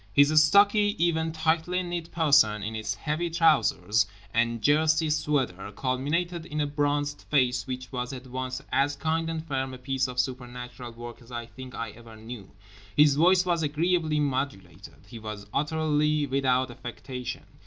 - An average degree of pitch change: Yes, average, 4.3 semitones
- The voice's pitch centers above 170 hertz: No, medium, 140 Hz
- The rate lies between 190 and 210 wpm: No, average, 160 wpm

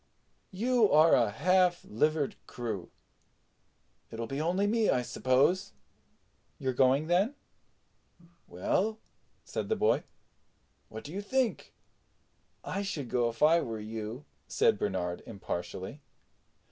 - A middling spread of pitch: No, wide, 8.4 semitones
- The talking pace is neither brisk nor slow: No, slow, 120 wpm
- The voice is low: No, medium, 150 Hz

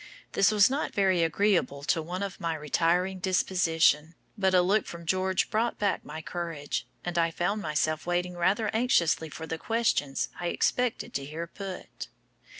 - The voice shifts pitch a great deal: No, average, 3.3 semitones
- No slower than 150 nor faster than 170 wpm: Yes, average, 165 wpm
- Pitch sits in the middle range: Yes, medium, 175 Hz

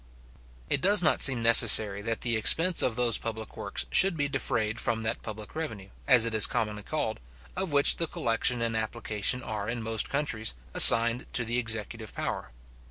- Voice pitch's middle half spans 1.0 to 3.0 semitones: Yes, narrow, 2.6 semitones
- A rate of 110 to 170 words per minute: No, average, 180 wpm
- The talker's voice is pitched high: No, low, 115 Hz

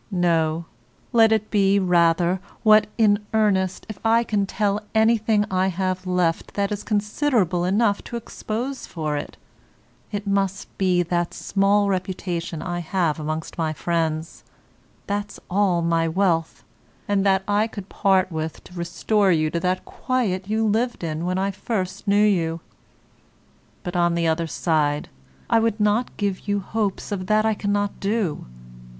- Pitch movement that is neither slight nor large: Yes, average, 3.4 semitones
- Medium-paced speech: Yes, average, 155 wpm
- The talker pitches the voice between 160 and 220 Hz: Yes, high, 190 Hz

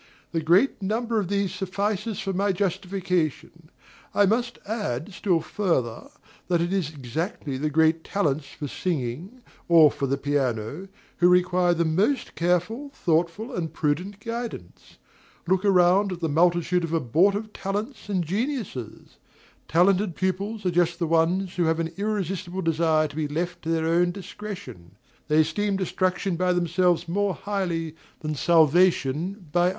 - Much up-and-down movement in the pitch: No, average, 3.6 semitones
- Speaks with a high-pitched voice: No, medium, 175 Hz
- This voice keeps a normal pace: Yes, average, 150 wpm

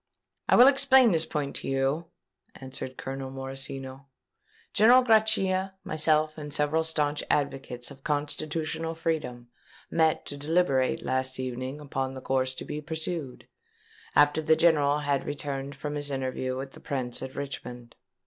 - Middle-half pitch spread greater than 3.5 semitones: No, average, 3.1 semitones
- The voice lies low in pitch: No, medium, 145 Hz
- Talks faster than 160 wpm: No, average, 145 wpm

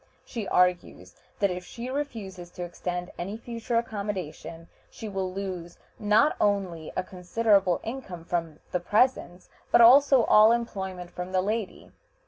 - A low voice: No, high, 195 Hz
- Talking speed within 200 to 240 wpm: No, average, 140 wpm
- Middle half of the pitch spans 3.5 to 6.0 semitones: Yes, average, 4.1 semitones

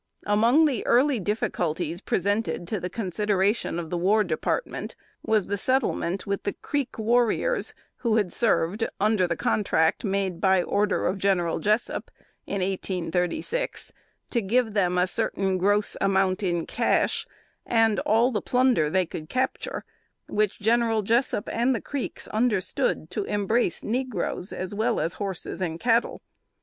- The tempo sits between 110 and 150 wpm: Yes, average, 145 wpm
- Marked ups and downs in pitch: No, average, 3.7 semitones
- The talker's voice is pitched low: No, high, 205 Hz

